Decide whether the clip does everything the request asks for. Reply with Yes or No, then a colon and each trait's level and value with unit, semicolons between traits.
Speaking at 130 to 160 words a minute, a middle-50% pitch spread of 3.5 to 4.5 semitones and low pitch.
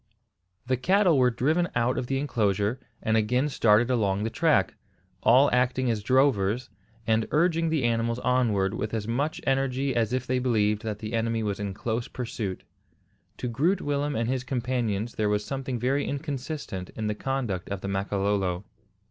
No: average, 175 wpm; average, 4.0 semitones; low, 120 Hz